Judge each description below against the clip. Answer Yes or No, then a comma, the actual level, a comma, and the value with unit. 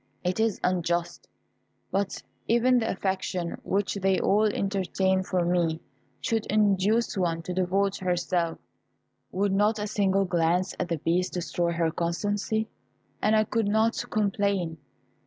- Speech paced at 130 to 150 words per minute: Yes, average, 140 wpm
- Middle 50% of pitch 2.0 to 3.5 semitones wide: Yes, average, 2.8 semitones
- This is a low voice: No, high, 190 Hz